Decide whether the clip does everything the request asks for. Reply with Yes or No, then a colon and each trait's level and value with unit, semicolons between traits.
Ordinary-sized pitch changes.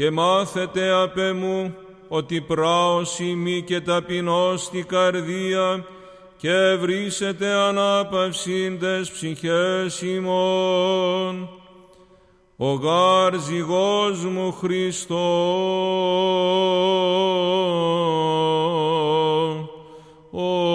No: narrow, 1.3 semitones